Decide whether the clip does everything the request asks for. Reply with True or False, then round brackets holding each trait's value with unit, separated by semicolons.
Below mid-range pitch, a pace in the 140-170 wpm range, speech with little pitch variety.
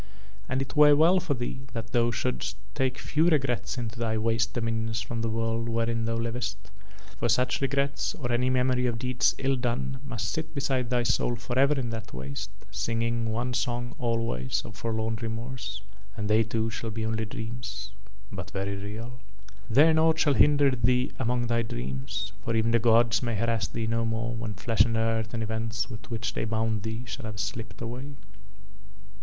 False (115 Hz; 185 wpm; 2.1 semitones)